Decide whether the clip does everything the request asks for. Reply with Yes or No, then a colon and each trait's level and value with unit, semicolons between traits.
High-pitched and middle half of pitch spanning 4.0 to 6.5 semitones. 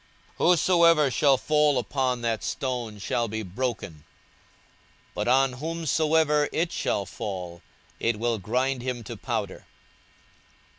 No: low, 125 Hz; average, 5.2 semitones